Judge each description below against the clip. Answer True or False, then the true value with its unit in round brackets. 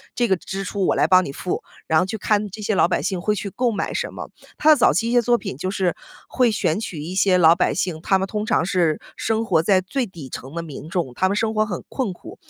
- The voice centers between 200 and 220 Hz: False (190 Hz)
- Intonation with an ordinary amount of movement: True (3.7 semitones)